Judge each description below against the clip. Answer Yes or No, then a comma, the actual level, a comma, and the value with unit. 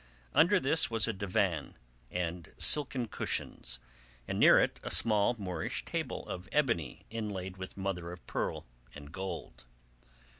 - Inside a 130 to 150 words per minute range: Yes, average, 140 wpm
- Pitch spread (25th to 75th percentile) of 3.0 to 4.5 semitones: Yes, average, 4.2 semitones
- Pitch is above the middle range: No, very low, 95 Hz